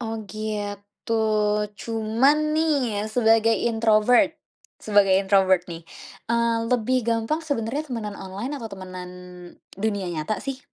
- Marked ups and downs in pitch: No, average, 2.7 semitones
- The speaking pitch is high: Yes, high, 220 Hz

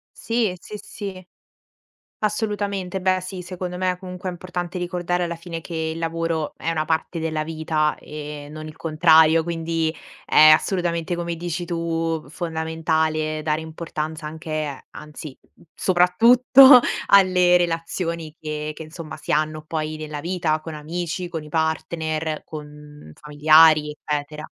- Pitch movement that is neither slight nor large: No, narrow, 2.3 semitones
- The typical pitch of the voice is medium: Yes, medium, 165 Hz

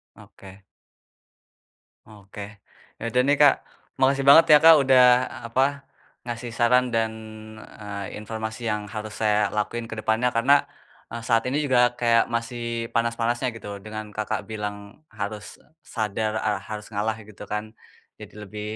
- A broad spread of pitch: No, narrow, 2.4 semitones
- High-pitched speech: No, low, 110 Hz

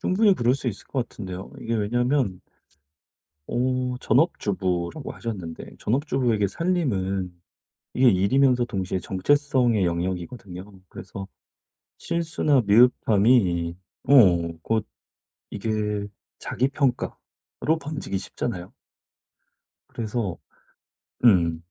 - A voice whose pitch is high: No, low, 115 Hz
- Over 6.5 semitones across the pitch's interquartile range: No, average, 5.2 semitones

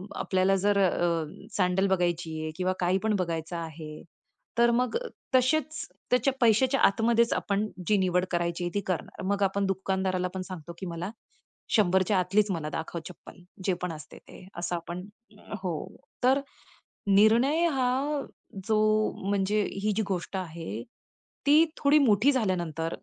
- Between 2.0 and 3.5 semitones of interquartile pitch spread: No, average, 4.1 semitones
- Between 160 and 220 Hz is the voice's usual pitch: Yes, high, 190 Hz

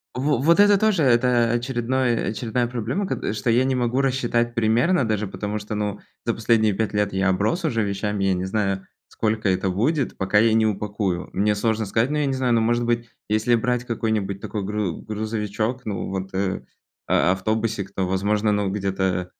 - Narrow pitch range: No, average, 3.1 semitones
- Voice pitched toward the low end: Yes, low, 110 Hz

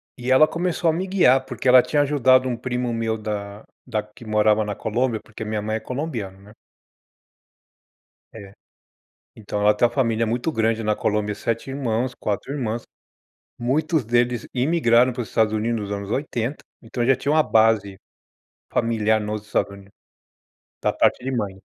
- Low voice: Yes, low, 115 Hz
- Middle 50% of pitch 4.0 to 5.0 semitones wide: No, average, 3.3 semitones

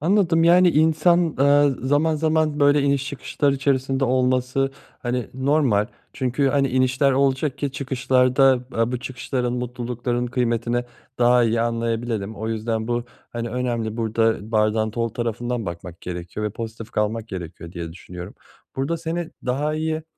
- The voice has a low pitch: Yes, low, 125 Hz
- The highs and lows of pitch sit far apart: No, average, 3.7 semitones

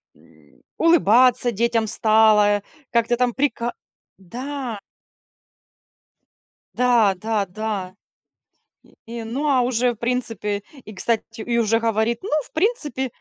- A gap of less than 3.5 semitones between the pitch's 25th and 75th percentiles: Yes, narrow, 2.6 semitones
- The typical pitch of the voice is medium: No, high, 230 Hz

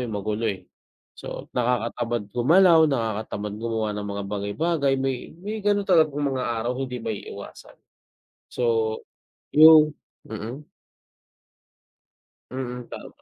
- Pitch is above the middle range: No, low, 125 Hz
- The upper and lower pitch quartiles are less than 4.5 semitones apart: No, wide, 5.4 semitones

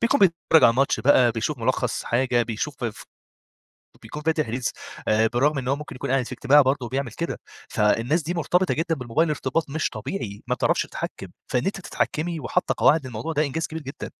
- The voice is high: No, medium, 140 Hz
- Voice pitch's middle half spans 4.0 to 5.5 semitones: Yes, average, 4.6 semitones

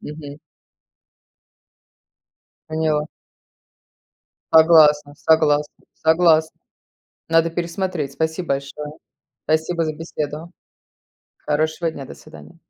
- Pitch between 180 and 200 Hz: No, medium, 155 Hz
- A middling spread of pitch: No, narrow, 1.6 semitones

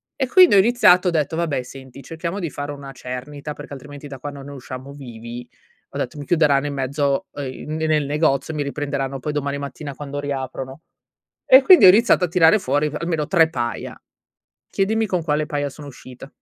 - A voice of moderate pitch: Yes, medium, 145 Hz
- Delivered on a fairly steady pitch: No, average, 3.0 semitones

